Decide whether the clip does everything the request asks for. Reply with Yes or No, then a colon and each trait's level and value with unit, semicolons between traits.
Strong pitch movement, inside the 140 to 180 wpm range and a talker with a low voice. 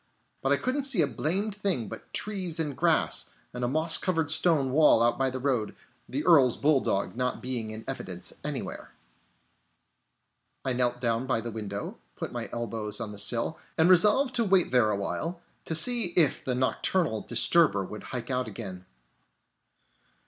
Yes: wide, 6.3 semitones; average, 170 wpm; low, 130 Hz